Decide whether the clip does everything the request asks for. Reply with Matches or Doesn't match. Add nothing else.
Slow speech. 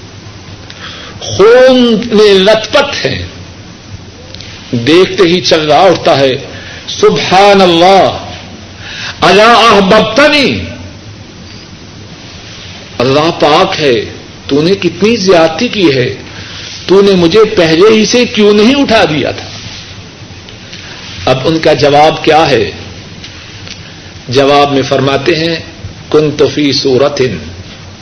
Matches